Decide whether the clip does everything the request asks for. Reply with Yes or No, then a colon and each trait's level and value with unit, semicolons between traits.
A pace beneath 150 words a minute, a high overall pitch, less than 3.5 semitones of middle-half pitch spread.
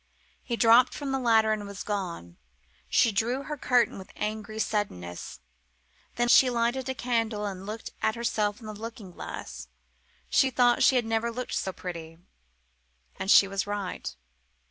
No: average, 160 wpm; high, 220 Hz; average, 3.1 semitones